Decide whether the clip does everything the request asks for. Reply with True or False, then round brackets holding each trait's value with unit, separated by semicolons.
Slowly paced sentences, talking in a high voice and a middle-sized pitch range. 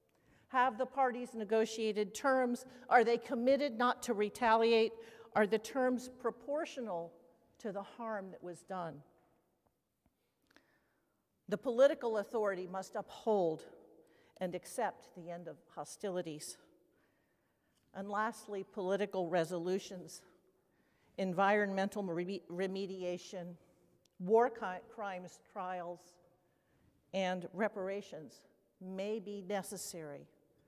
True (95 wpm; 200 Hz; 4.0 semitones)